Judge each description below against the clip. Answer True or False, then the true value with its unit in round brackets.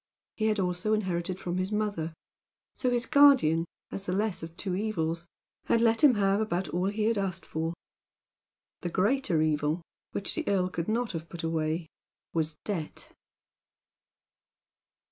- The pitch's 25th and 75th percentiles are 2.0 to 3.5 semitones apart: False (4.5 semitones)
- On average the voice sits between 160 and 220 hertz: True (185 Hz)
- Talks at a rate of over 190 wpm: False (155 wpm)